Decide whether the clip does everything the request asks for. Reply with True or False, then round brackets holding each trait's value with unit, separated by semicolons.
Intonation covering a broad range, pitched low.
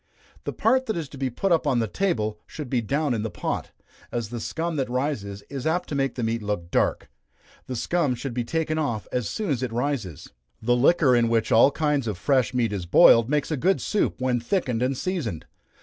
False (4.8 semitones; 130 Hz)